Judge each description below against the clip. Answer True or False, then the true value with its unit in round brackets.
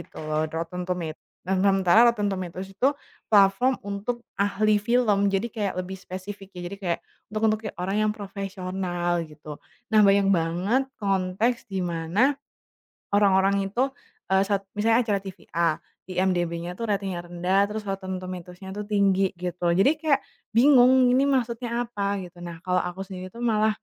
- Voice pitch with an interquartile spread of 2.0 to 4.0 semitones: True (2.8 semitones)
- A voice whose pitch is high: True (195 Hz)